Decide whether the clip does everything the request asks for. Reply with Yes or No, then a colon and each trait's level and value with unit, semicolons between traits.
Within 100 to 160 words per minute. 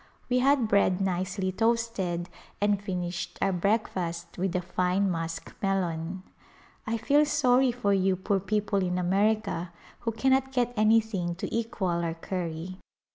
Yes: average, 140 wpm